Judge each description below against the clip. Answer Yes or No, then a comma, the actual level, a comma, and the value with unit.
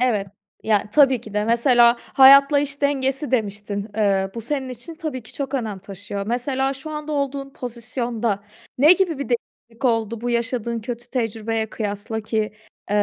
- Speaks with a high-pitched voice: Yes, high, 240 Hz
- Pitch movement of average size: Yes, average, 3.7 semitones